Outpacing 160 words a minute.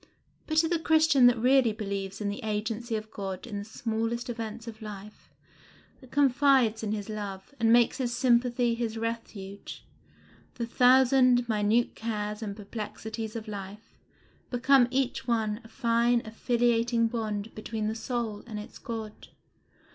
No: average, 150 wpm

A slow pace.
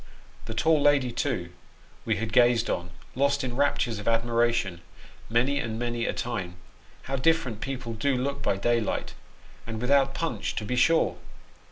No: average, 160 wpm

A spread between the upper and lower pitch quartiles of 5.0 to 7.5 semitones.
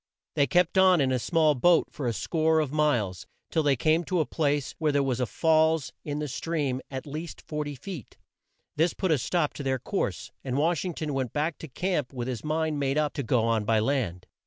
No: average, 3.5 semitones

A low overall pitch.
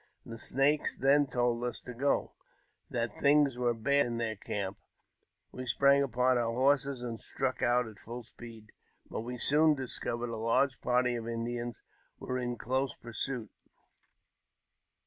Yes: low, 120 Hz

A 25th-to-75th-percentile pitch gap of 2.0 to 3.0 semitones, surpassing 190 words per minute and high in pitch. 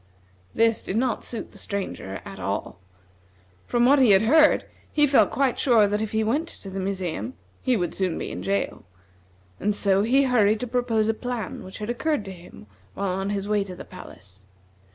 No: average, 4.4 semitones; average, 200 wpm; high, 215 Hz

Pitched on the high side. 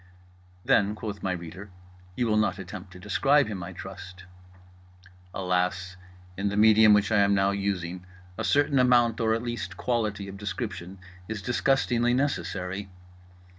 No: low, 100 Hz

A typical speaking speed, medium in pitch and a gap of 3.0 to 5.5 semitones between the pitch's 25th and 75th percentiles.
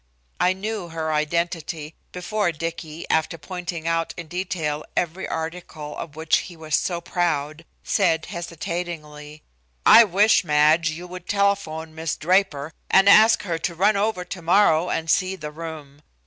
No: average, 150 wpm; medium, 165 Hz; narrow, 2.6 semitones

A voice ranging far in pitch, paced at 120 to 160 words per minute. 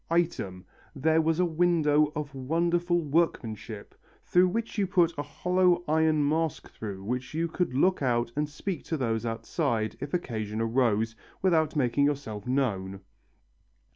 Yes: wide, 6.4 semitones; average, 145 wpm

